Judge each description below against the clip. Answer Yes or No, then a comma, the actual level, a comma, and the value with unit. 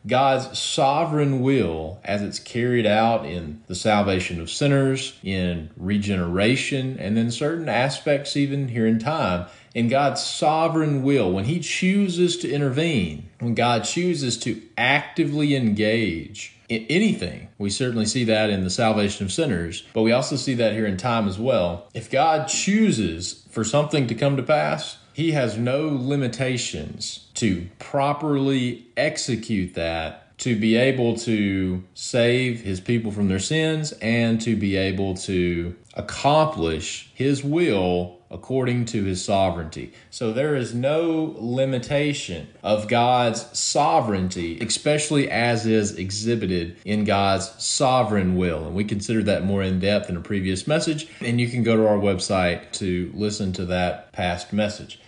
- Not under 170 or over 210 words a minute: No, average, 150 wpm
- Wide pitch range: Yes, wide, 5.7 semitones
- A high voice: No, low, 115 Hz